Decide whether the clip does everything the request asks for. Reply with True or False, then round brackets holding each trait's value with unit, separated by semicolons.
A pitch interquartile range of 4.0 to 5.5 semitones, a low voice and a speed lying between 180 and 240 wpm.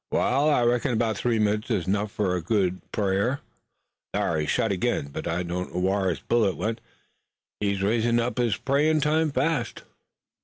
True (4.4 semitones; 110 Hz; 185 wpm)